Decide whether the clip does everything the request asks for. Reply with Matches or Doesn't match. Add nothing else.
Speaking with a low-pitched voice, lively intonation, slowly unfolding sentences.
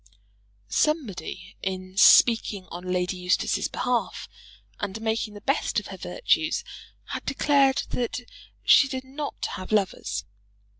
Doesn't match